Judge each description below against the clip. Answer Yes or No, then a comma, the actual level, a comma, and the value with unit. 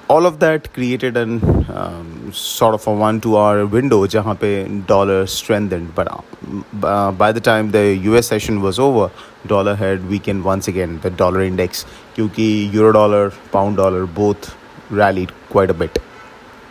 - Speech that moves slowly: No, average, 145 wpm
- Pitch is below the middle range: Yes, low, 100 Hz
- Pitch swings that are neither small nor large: No, narrow, 2.3 semitones